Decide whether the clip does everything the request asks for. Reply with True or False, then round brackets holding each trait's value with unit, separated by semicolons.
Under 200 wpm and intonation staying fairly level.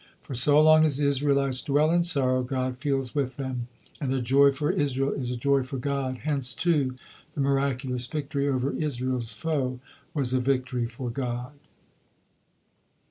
True (165 wpm; 2.0 semitones)